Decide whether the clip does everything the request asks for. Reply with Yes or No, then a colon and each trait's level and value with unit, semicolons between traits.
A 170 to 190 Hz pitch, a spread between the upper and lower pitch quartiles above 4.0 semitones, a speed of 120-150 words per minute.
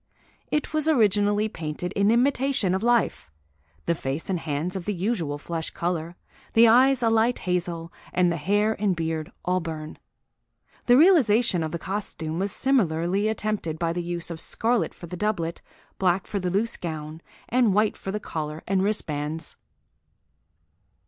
No: medium, 185 Hz; average, 4.8 semitones; average, 160 wpm